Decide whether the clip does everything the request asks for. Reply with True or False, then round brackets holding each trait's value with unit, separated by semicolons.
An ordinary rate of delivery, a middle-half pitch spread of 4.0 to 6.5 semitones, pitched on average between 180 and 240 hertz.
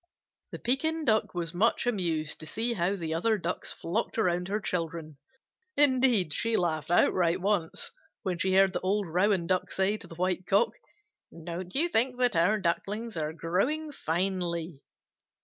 True (165 wpm; 4.7 semitones; 185 Hz)